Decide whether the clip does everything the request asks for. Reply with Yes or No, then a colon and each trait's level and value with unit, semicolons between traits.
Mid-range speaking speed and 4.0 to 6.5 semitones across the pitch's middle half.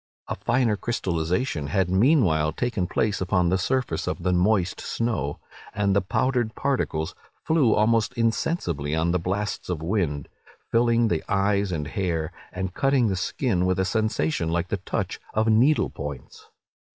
Yes: average, 155 wpm; average, 5.1 semitones